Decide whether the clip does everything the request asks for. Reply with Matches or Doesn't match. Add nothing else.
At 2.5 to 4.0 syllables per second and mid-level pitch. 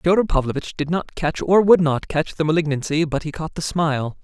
Doesn't match